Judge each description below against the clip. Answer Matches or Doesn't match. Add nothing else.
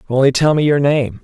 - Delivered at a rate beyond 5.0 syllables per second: Matches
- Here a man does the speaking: Matches